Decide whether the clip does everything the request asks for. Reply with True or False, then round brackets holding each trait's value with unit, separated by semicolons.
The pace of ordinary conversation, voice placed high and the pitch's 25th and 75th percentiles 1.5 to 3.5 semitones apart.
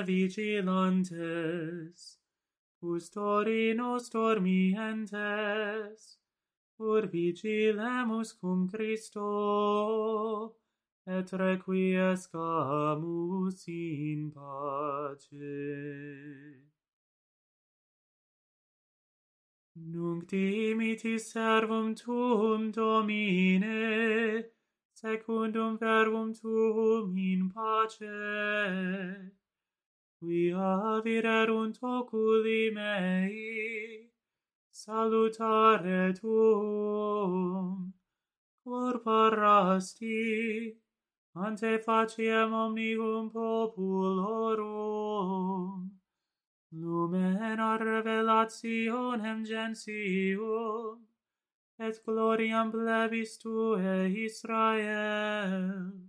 False (45 wpm; 215 Hz; 3.0 semitones)